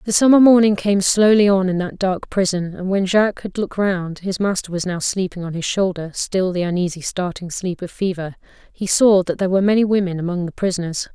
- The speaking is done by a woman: Yes, female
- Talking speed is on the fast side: Yes, fast, 210 wpm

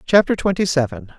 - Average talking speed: Yes, average, 150 wpm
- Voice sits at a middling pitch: Yes, medium, 175 Hz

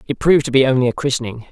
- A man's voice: Yes, male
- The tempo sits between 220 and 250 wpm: No, fast, 275 wpm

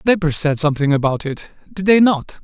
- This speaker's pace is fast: Yes, fast, 220 wpm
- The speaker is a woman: No, male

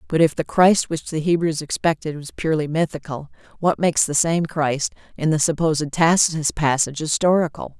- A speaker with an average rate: Yes, average, 170 wpm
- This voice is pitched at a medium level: Yes, medium, 155 Hz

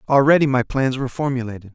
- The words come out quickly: No, average, 170 wpm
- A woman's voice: No, male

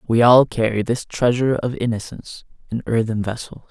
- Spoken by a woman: No, male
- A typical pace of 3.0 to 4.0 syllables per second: No, 5.1 syllables/s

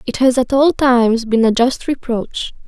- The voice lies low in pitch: No, high, 245 Hz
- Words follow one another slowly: No, average, 200 wpm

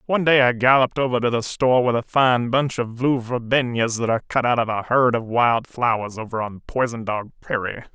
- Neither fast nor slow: No, fast, 225 wpm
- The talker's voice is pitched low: Yes, low, 120 Hz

